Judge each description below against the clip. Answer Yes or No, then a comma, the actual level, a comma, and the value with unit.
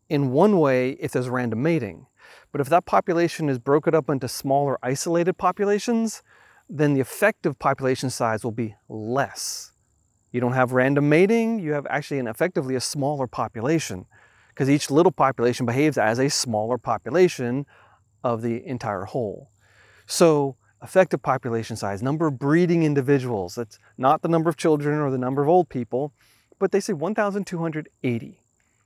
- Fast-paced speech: No, average, 160 wpm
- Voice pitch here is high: No, medium, 140 Hz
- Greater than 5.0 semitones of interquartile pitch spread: Yes, wide, 5.5 semitones